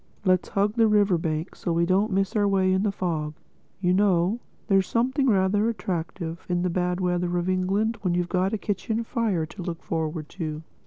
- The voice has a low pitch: No, medium, 185 Hz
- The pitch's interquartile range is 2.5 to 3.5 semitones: Yes, average, 2.9 semitones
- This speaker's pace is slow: No, average, 195 wpm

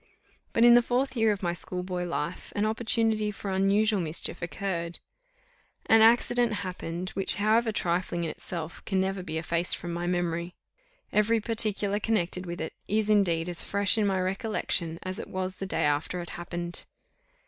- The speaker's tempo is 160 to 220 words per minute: Yes, average, 170 wpm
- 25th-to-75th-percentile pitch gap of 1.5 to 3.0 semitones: No, average, 3.7 semitones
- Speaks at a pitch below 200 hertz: Yes, high, 190 Hz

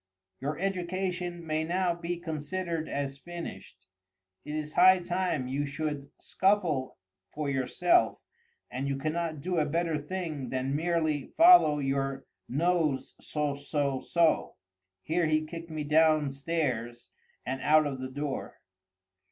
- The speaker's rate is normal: No, slow, 120 wpm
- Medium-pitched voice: Yes, medium, 155 Hz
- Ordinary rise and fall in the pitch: Yes, average, 3.8 semitones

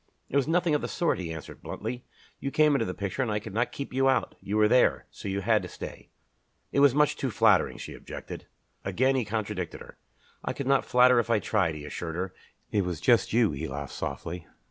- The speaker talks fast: Yes, fast, 235 wpm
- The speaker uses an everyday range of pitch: No, wide, 6.2 semitones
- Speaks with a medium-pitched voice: No, low, 110 Hz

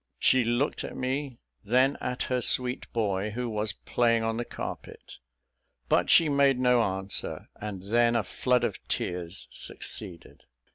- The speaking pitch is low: Yes, low, 120 Hz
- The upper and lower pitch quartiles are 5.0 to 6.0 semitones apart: No, average, 3.3 semitones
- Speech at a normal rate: Yes, average, 150 wpm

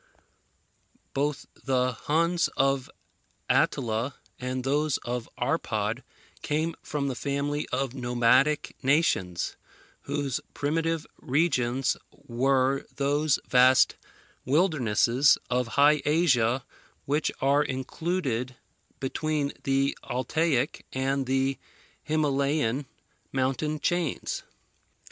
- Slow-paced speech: Yes, slow, 90 wpm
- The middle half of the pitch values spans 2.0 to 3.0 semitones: Yes, average, 2.7 semitones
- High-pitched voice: No, low, 135 Hz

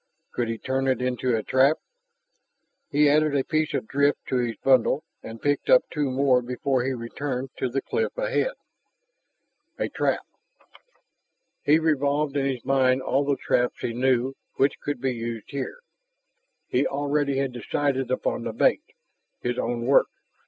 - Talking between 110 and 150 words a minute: No, average, 160 wpm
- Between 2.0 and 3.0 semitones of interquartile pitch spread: Yes, narrow, 2.4 semitones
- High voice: No, low, 135 Hz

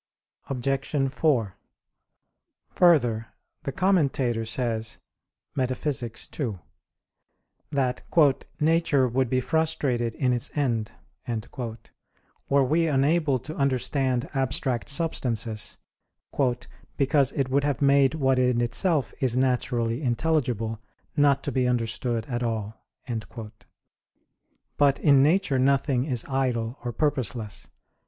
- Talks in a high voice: No, low, 130 Hz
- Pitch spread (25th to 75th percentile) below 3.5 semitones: Yes, average, 3.0 semitones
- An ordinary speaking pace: No, slow, 105 wpm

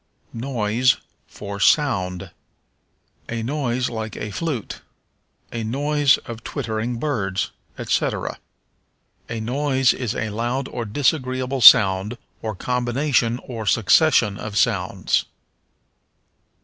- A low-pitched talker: Yes, low, 120 Hz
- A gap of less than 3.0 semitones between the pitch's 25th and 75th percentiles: No, average, 3.4 semitones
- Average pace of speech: No, slow, 100 wpm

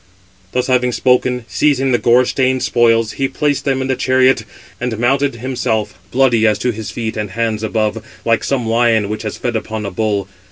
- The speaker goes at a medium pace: Yes, average, 195 wpm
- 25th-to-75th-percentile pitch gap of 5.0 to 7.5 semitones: No, average, 2.7 semitones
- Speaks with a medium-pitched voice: No, low, 120 Hz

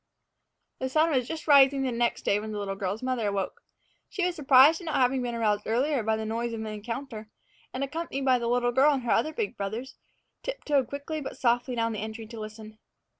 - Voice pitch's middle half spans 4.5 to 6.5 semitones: No, average, 4.1 semitones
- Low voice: No, high, 245 Hz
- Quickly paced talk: Yes, fast, 220 wpm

